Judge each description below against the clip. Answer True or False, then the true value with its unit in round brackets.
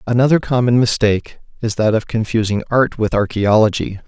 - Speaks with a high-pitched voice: False (115 Hz)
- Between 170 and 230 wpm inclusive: False (145 wpm)